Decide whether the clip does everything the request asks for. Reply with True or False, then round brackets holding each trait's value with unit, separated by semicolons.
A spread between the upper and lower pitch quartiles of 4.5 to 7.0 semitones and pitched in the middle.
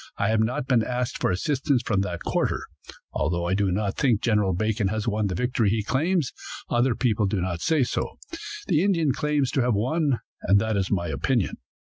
False (5.0 semitones; 110 Hz)